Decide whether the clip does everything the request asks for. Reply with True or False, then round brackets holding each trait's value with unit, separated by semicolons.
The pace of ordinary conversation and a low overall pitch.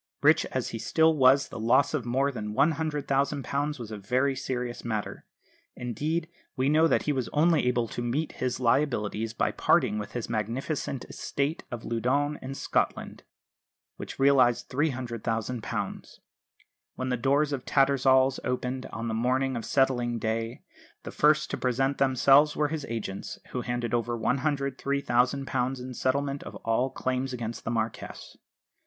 True (150 wpm; 130 Hz)